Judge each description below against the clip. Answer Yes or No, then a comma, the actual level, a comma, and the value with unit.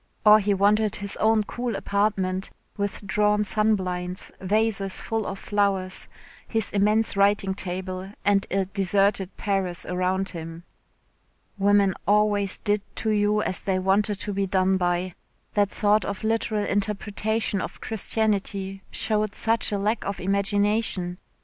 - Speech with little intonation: Yes, narrow, 1.8 semitones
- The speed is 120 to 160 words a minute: Yes, slow, 135 wpm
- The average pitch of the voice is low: No, high, 200 Hz